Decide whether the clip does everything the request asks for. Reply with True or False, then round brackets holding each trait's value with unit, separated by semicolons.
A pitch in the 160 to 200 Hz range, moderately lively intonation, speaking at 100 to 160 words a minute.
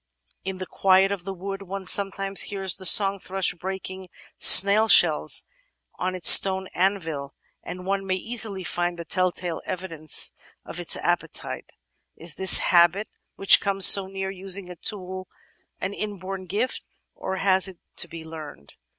False (190 Hz; 1.6 semitones; 155 wpm)